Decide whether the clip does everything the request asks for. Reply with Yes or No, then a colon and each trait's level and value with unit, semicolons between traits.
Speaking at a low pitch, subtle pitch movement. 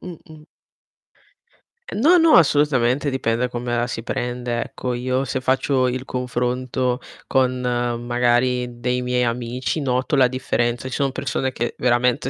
Yes: low, 125 Hz; narrow, 1.4 semitones